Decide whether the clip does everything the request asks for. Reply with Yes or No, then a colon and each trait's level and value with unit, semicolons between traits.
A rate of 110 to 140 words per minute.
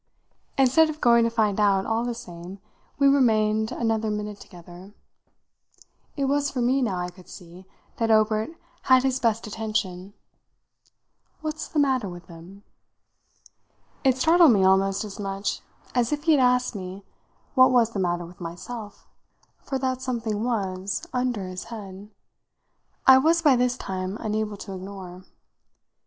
No: average, 150 wpm